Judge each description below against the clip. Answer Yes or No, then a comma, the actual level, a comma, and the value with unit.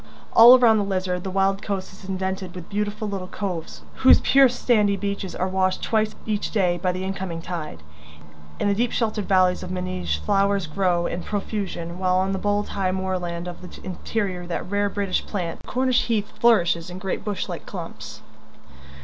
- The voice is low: No, high, 190 Hz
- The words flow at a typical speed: Yes, average, 185 wpm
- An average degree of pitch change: No, narrow, 2.2 semitones